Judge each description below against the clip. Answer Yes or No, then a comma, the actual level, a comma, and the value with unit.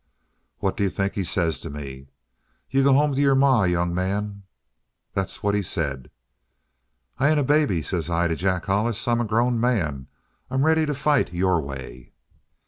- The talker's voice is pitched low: Yes, low, 100 Hz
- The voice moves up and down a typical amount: No, wide, 7.6 semitones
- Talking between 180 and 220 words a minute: Yes, average, 185 wpm